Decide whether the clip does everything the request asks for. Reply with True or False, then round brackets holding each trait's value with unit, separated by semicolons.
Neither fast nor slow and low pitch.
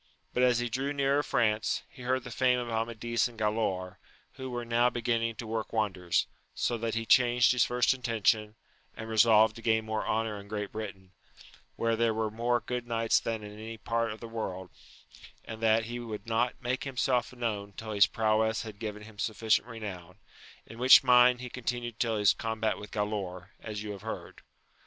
True (195 wpm; 115 Hz)